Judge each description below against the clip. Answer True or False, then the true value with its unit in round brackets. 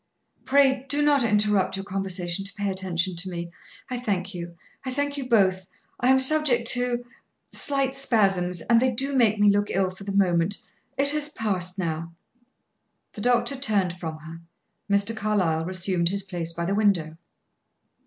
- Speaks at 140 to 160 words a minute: False (170 wpm)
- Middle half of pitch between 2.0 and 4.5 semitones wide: False (5.4 semitones)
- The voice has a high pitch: True (200 Hz)